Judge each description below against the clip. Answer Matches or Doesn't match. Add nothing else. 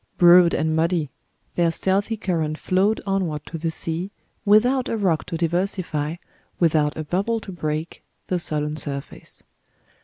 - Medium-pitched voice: Matches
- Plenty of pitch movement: Doesn't match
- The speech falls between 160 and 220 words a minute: Doesn't match